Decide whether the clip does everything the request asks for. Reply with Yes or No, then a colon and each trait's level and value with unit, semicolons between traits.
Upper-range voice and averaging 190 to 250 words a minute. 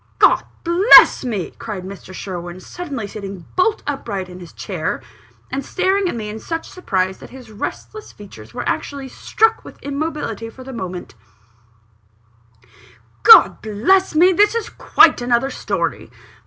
No: high, 235 Hz; average, 150 wpm